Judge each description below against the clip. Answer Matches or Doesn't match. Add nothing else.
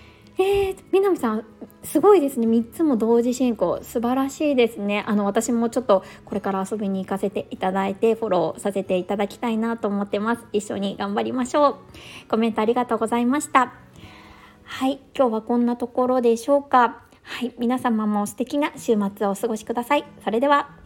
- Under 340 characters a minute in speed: Doesn't match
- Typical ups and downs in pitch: Matches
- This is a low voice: Doesn't match